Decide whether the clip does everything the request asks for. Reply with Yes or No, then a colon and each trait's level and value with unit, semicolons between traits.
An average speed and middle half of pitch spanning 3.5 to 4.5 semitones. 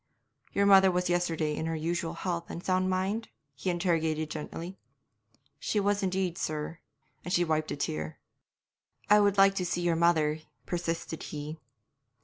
No: average, 155 wpm; average, 2.8 semitones